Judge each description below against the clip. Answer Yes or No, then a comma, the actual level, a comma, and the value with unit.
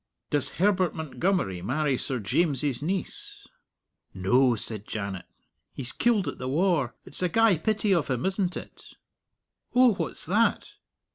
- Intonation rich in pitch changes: Yes, wide, 7.1 semitones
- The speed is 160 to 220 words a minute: No, average, 140 wpm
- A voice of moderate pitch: Yes, medium, 155 Hz